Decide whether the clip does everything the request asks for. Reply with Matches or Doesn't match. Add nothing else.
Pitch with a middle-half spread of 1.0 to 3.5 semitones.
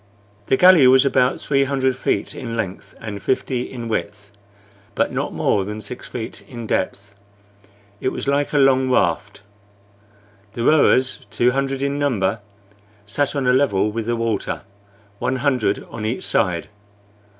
Doesn't match